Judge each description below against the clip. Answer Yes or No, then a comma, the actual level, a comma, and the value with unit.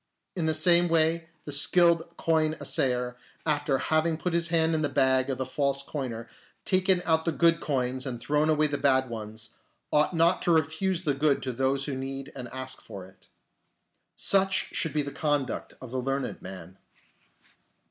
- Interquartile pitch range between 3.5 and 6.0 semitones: Yes, average, 3.8 semitones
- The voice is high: No, medium, 145 Hz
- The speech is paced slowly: No, average, 180 wpm